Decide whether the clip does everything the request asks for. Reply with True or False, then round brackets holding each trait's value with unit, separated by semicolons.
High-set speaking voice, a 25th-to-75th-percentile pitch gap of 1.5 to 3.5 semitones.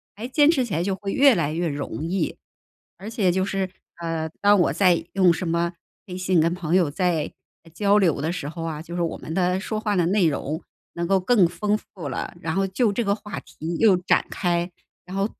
False (180 Hz; 3.1 semitones)